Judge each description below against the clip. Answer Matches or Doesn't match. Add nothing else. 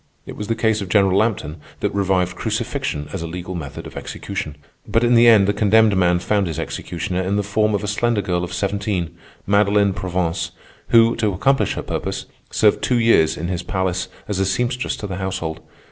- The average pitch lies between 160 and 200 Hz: Doesn't match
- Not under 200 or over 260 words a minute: Matches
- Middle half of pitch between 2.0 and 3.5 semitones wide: Matches